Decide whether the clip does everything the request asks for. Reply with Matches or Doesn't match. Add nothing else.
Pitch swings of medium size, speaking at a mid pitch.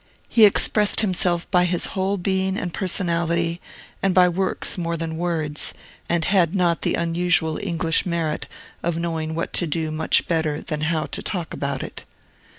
Doesn't match